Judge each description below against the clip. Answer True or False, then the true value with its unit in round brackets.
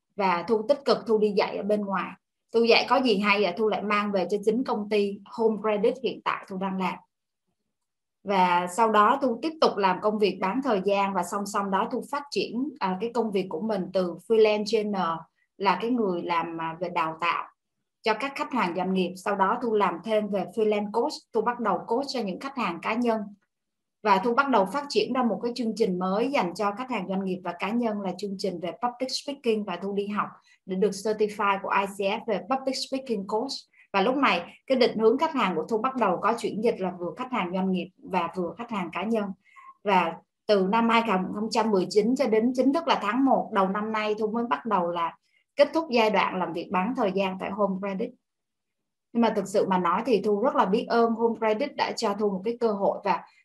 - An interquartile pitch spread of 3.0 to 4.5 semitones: True (3.6 semitones)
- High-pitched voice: True (215 Hz)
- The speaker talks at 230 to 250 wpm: True (235 wpm)